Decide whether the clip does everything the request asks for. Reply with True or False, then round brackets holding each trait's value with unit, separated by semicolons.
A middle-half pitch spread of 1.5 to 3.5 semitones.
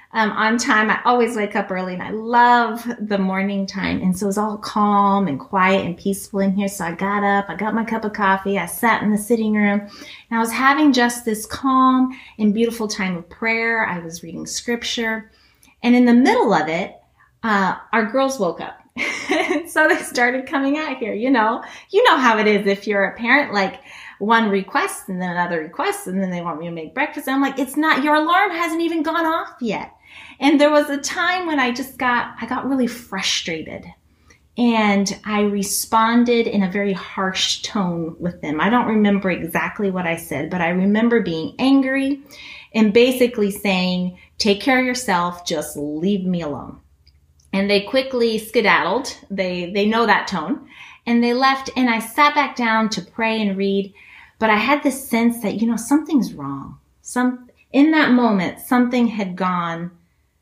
False (4.8 semitones)